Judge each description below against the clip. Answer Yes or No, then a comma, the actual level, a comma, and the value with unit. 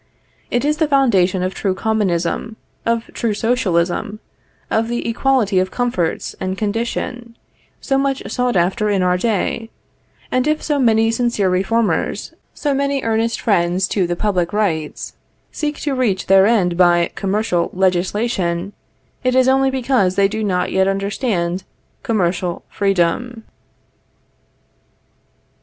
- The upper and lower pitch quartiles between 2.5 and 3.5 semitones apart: No, average, 4.7 semitones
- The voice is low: No, high, 210 Hz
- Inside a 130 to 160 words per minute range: Yes, slow, 135 wpm